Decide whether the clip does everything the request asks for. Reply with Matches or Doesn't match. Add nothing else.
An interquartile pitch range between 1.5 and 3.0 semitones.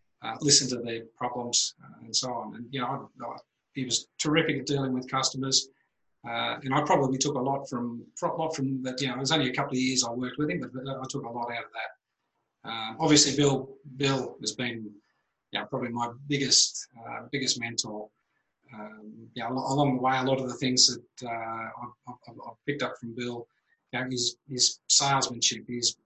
Matches